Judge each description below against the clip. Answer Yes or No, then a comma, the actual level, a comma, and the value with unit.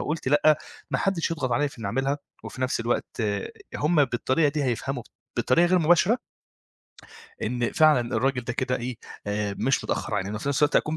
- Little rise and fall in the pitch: No, average, 4.1 semitones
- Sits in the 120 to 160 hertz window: Yes, low, 135 Hz